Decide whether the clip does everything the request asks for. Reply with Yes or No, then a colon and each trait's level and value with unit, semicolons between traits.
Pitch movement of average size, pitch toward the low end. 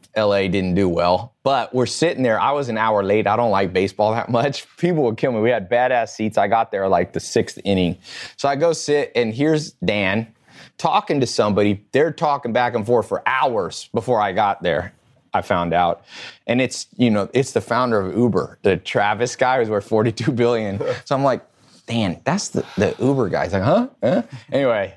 Yes: average, 3.7 semitones; low, 115 Hz